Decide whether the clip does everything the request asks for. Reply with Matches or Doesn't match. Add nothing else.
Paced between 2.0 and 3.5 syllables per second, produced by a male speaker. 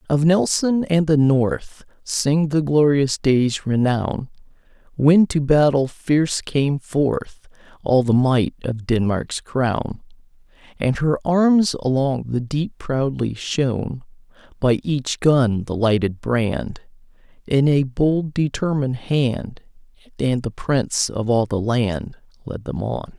Matches